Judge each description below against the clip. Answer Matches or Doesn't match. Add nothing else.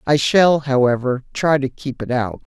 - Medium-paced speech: Matches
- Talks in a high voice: Doesn't match